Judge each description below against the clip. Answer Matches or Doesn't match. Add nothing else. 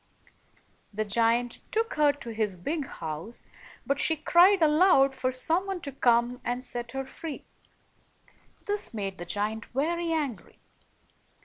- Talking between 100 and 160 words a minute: Matches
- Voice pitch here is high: Matches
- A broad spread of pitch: Matches